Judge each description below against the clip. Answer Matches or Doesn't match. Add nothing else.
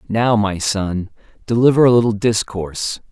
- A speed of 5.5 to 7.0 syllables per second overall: Doesn't match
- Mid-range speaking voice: Doesn't match